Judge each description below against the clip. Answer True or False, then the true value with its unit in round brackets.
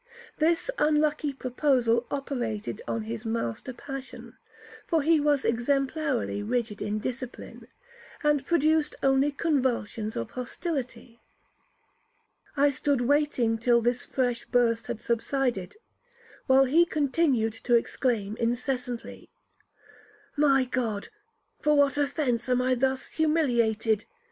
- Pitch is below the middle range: False (255 Hz)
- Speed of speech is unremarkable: False (110 wpm)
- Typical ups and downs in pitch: True (3.7 semitones)